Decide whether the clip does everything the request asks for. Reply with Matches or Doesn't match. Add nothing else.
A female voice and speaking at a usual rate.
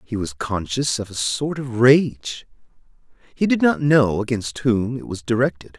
Doesn't match